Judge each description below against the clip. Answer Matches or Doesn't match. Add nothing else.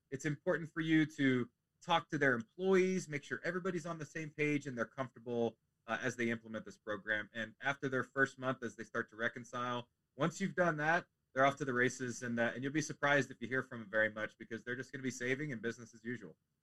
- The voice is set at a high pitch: Doesn't match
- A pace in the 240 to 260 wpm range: Matches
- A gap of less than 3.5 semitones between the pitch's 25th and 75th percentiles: Doesn't match